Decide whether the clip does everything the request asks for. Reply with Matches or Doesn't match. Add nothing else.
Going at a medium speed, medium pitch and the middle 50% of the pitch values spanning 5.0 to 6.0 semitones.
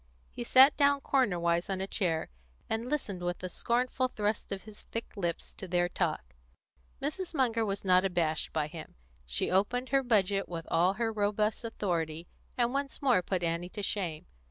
Doesn't match